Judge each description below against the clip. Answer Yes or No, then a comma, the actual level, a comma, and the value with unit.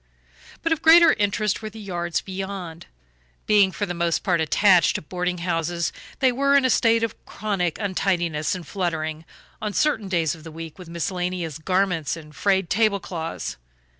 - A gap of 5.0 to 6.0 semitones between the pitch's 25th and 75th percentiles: No, average, 3.7 semitones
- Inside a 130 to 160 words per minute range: No, average, 170 wpm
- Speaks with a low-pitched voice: No, medium, 180 Hz